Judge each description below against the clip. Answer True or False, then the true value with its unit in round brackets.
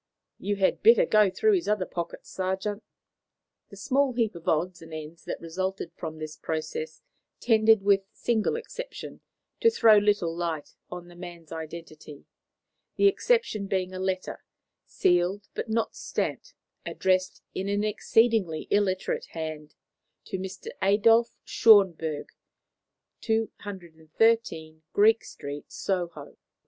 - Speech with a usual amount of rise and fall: True (4.7 semitones)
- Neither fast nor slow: False (130 wpm)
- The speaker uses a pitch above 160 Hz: True (190 Hz)